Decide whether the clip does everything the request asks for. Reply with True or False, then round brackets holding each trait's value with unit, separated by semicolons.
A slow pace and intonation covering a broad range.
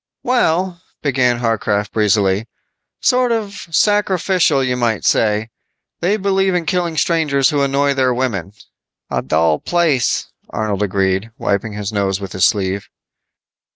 True (130 wpm; 8.9 semitones)